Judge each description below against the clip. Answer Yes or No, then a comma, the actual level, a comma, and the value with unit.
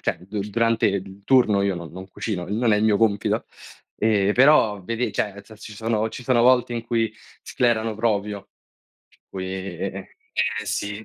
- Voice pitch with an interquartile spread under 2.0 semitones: No, narrow, 2.5 semitones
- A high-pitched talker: No, low, 105 Hz